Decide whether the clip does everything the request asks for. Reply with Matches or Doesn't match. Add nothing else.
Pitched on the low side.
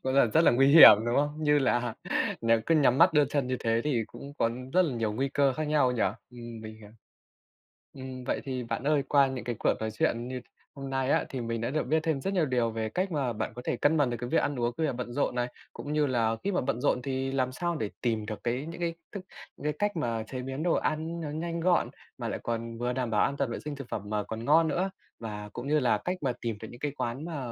Matches